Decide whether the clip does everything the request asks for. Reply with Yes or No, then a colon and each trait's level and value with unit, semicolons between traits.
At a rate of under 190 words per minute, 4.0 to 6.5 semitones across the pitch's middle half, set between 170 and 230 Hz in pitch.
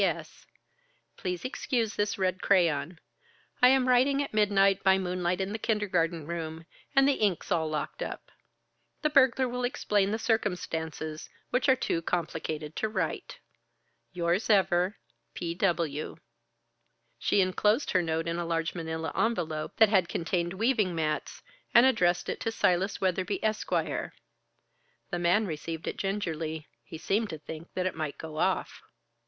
Yes: average, 155 wpm; average, 4.6 semitones; medium, 185 Hz